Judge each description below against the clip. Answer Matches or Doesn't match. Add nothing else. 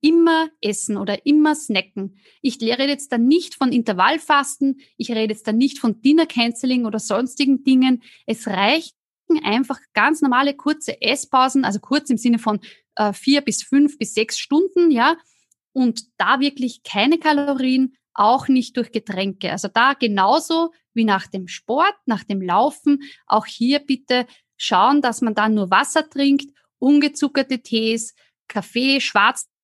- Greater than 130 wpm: Matches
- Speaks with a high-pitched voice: Matches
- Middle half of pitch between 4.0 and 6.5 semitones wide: Matches